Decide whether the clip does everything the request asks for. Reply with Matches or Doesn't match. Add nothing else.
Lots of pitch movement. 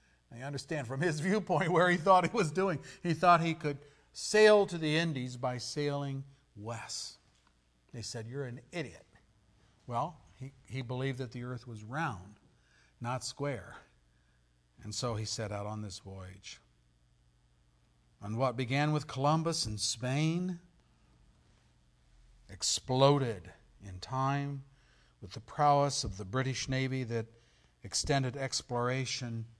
Matches